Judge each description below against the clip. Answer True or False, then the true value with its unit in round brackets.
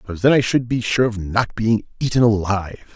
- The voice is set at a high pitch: False (110 Hz)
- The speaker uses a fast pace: True (225 wpm)